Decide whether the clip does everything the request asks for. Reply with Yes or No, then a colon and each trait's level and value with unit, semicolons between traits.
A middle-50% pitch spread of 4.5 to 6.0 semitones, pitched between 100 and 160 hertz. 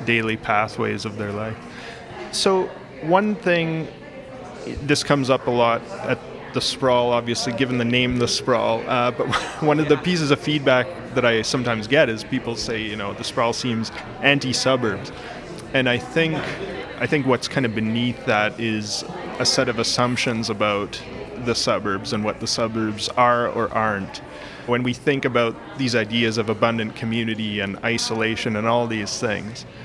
No: average, 2.8 semitones; low, 120 Hz